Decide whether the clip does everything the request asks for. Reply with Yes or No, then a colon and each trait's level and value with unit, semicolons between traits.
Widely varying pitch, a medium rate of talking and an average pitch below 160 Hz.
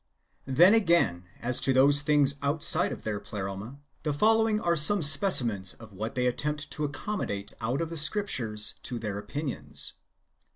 Yes: wide, 6.5 semitones; average, 160 wpm; medium, 140 Hz